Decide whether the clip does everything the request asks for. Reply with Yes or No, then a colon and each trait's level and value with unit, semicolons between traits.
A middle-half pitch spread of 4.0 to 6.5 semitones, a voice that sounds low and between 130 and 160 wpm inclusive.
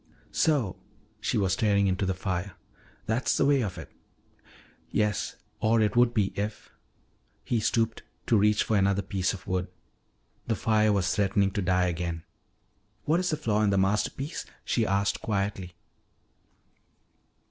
No: average, 2.8 semitones; low, 100 Hz; average, 155 wpm